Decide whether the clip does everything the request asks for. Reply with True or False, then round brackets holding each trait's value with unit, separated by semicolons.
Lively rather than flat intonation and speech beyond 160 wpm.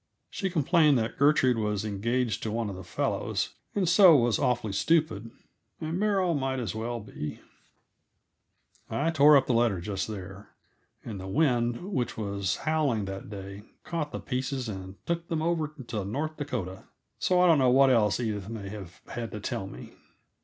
True (6.8 semitones; 175 wpm)